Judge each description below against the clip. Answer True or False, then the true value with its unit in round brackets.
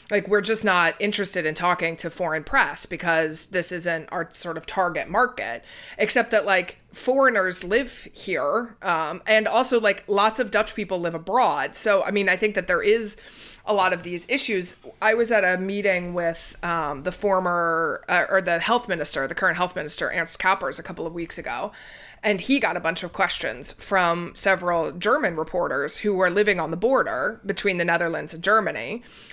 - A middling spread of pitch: True (3.6 semitones)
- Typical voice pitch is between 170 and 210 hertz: True (185 Hz)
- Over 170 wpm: True (190 wpm)